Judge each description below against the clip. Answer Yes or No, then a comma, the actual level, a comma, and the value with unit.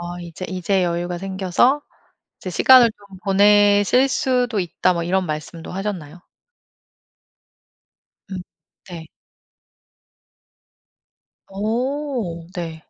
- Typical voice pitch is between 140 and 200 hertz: Yes, high, 190 Hz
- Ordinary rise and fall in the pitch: Yes, average, 3.4 semitones